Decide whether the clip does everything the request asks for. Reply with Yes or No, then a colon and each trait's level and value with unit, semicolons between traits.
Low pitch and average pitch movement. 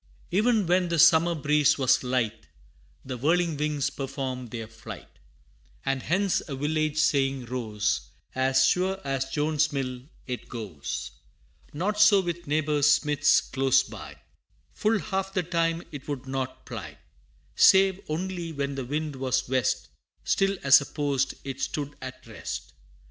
No: medium, 145 Hz; average, 4.2 semitones